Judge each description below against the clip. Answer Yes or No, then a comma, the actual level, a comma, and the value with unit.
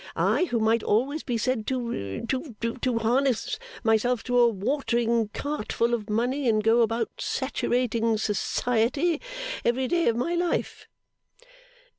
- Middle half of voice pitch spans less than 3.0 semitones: Yes, narrow, 2.6 semitones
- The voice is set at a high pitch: Yes, high, 235 Hz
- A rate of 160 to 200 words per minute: No, average, 140 wpm